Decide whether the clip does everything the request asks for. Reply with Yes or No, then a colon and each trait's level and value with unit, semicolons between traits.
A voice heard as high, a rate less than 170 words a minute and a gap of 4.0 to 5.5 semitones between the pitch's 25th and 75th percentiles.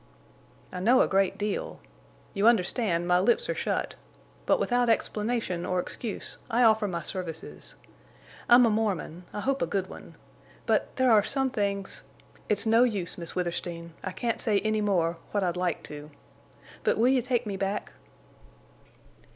Yes: high, 205 Hz; average, 155 wpm; average, 4.3 semitones